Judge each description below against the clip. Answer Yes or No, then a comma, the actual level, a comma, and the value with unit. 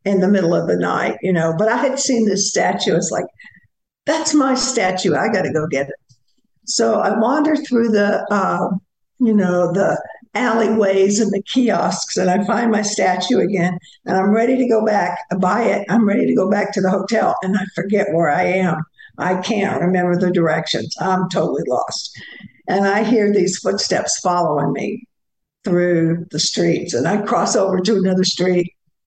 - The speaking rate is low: No, average, 190 wpm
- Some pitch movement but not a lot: Yes, average, 3.7 semitones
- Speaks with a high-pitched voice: Yes, high, 195 Hz